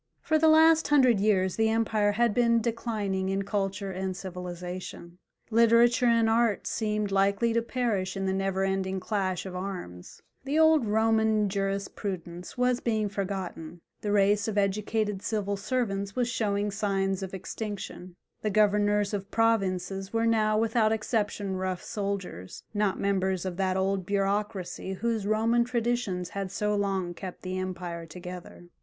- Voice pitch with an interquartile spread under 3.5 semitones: Yes, average, 2.8 semitones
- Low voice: No, high, 200 Hz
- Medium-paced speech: Yes, average, 150 wpm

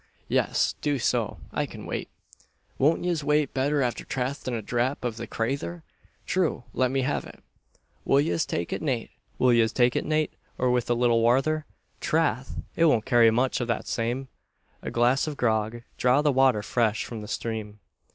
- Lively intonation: No, average, 3.5 semitones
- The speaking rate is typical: Yes, average, 170 wpm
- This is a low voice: Yes, low, 125 Hz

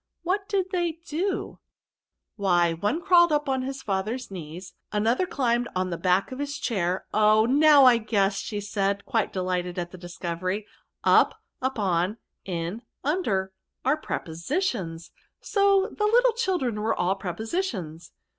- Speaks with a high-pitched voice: Yes, high, 215 Hz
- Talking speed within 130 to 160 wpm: Yes, average, 155 wpm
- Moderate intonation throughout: No, wide, 8.5 semitones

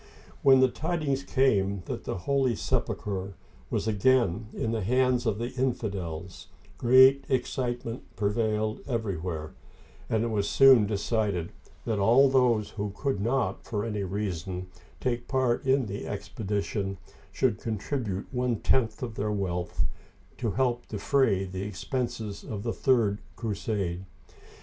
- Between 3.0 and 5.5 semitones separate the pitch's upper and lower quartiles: Yes, average, 4.2 semitones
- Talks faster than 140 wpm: No, slow, 135 wpm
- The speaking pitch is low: Yes, low, 110 Hz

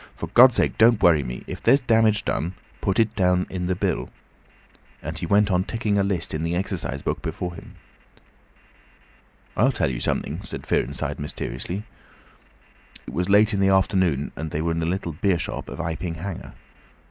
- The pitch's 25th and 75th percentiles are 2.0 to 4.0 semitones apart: Yes, average, 3.6 semitones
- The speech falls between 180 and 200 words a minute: Yes, average, 185 wpm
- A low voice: Yes, very low, 90 Hz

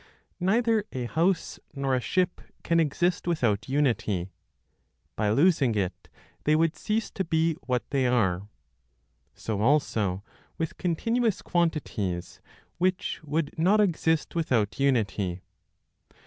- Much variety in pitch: Yes, wide, 7.7 semitones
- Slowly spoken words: Yes, slow, 120 wpm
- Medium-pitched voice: Yes, medium, 145 Hz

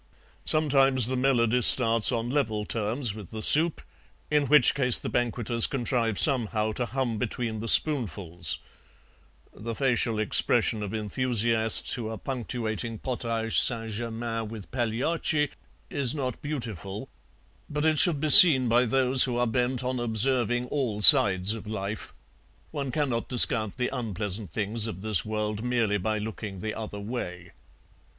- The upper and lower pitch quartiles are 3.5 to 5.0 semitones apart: No, average, 3.0 semitones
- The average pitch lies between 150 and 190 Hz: No, low, 115 Hz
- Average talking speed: Yes, average, 145 wpm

